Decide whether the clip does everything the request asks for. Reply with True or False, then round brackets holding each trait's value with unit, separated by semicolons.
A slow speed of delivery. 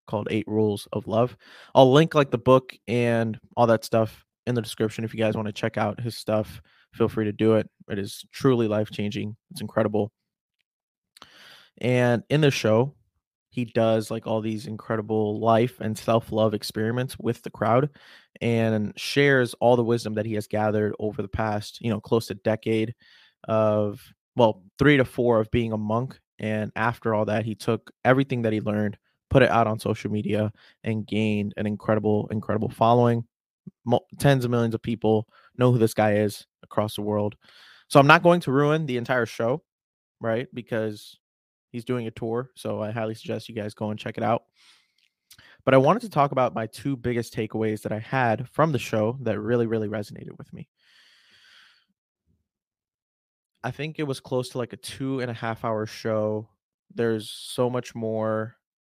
False (185 wpm)